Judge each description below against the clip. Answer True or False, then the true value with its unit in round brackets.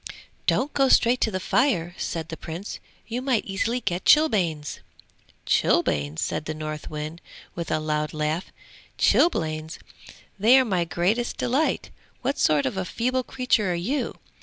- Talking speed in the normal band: True (150 wpm)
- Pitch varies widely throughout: True (7.9 semitones)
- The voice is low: False (185 Hz)